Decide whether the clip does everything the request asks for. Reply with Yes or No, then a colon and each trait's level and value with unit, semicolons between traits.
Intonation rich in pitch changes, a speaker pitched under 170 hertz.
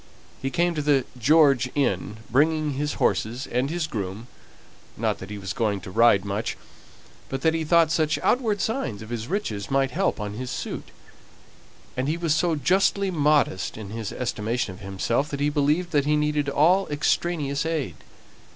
Yes: wide, 5.8 semitones; medium, 140 Hz